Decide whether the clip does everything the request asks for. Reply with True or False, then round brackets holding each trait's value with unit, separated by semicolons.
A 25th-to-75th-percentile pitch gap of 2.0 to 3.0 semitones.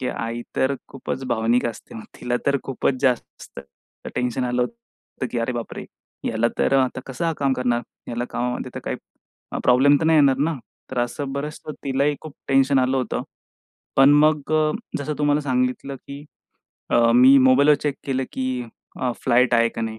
True (2.4 semitones)